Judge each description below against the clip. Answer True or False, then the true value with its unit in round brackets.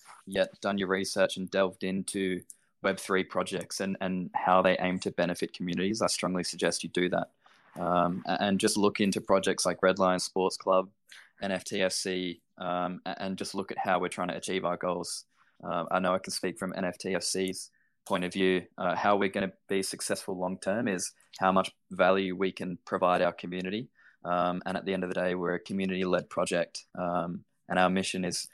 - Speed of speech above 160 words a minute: True (200 wpm)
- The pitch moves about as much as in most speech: False (1.1 semitones)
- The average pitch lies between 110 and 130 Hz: False (95 Hz)